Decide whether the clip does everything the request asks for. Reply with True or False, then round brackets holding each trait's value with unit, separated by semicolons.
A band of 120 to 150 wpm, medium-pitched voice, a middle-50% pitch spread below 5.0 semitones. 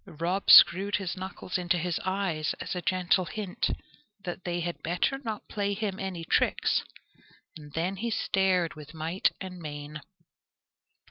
True (145 wpm; 180 Hz; 2.5 semitones)